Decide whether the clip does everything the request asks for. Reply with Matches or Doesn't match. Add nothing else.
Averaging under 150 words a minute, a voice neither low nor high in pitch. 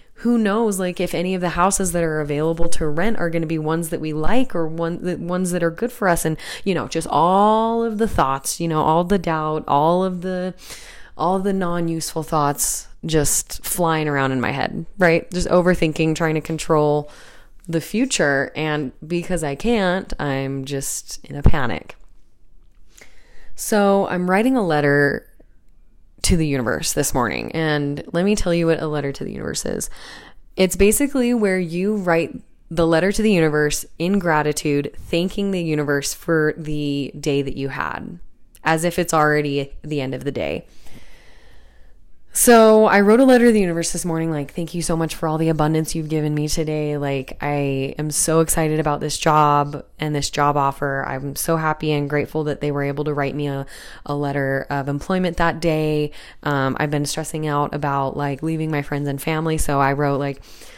Doesn't match